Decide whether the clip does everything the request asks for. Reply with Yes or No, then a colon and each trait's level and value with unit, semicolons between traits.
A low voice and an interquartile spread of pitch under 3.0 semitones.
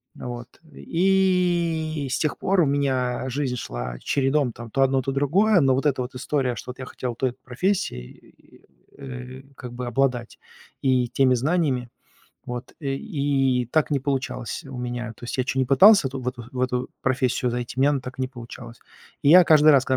Yes: low, 130 Hz; narrow, 2.6 semitones